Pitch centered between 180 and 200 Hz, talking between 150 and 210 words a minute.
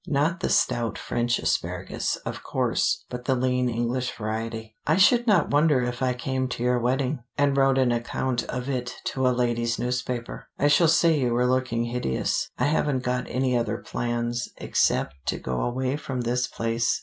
No: low, 125 Hz; average, 185 wpm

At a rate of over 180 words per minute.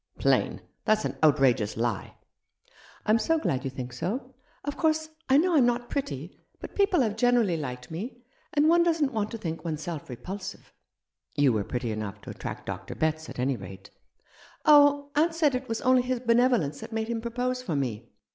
Yes: average, 195 wpm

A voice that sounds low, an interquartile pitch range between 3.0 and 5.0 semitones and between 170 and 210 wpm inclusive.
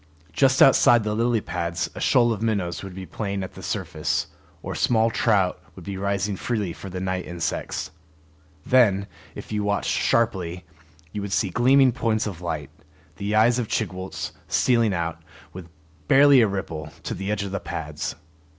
Yes: low, 100 Hz; average, 3.8 semitones; average, 175 wpm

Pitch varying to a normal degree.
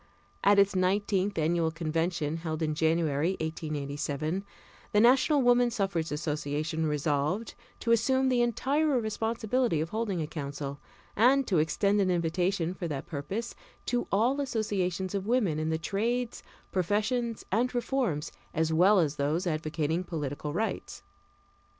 No: wide, 6.2 semitones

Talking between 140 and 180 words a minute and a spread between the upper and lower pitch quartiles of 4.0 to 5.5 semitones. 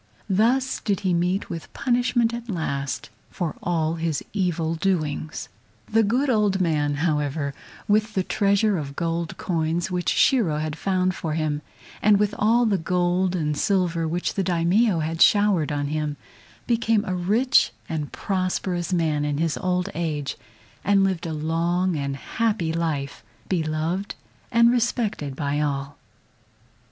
Yes: average, 150 wpm; average, 4.4 semitones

